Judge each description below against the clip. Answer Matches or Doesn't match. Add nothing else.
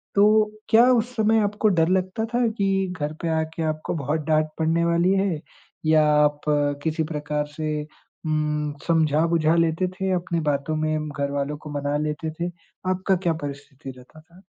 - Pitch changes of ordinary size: Matches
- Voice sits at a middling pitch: Matches